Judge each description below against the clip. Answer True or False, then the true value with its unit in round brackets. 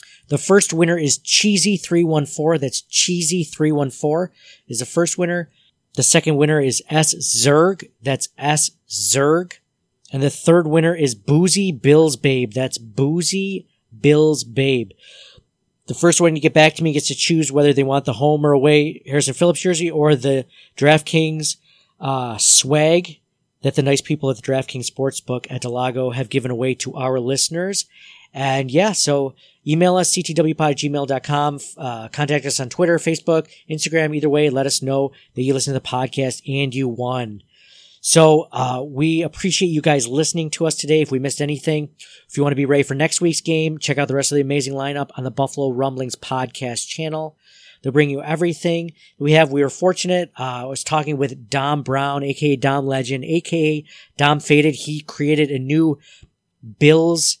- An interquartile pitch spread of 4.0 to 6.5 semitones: False (3.0 semitones)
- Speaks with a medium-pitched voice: True (150 Hz)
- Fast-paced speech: False (175 wpm)